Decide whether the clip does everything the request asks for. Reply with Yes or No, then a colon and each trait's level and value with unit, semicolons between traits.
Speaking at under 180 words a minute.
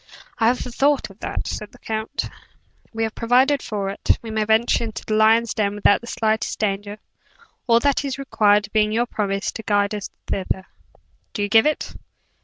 No: average, 190 wpm